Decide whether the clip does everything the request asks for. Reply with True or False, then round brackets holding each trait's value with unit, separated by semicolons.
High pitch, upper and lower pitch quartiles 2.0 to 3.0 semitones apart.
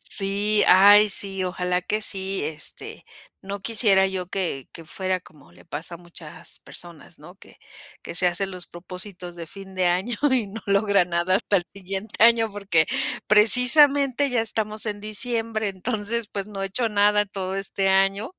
True (195 Hz; 2.7 semitones)